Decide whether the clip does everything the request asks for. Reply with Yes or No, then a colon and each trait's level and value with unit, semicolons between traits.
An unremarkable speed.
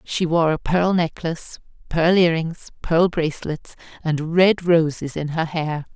Yes: average, 160 wpm